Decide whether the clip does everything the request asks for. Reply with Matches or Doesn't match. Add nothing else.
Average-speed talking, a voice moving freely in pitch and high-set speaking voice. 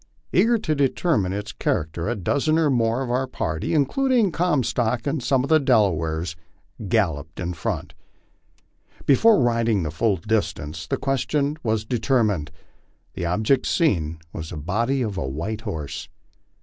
Doesn't match